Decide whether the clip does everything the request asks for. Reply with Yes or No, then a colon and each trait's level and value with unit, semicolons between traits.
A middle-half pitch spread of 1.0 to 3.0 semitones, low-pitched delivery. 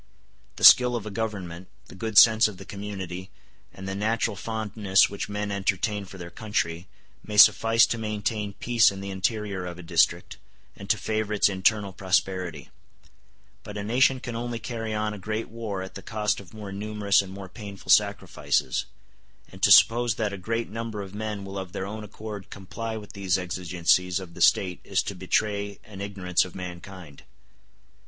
Yes: narrow, 2.4 semitones; low, 100 Hz